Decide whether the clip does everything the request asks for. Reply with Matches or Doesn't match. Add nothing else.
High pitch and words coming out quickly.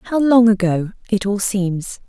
Doesn't match